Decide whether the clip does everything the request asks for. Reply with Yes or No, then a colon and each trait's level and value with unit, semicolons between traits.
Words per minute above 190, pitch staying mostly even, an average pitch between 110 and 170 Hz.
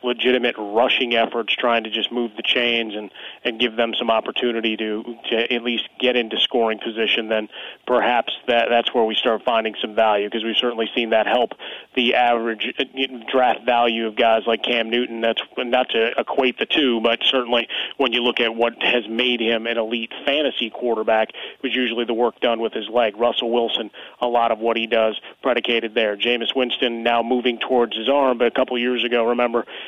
Yes: average, 200 wpm; narrow, 1.3 semitones; low, 120 Hz